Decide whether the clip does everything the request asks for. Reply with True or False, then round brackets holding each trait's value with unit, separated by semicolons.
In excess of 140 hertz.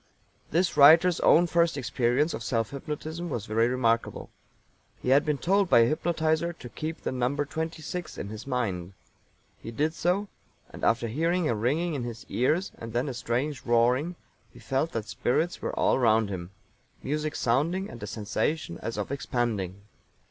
False (135 Hz)